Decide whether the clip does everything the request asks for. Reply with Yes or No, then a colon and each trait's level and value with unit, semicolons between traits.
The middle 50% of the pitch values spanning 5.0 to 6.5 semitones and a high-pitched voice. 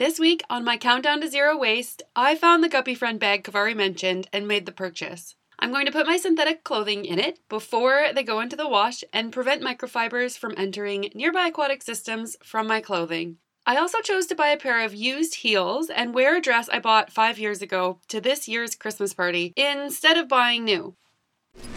Yes: wide, 5.6 semitones; high, 235 Hz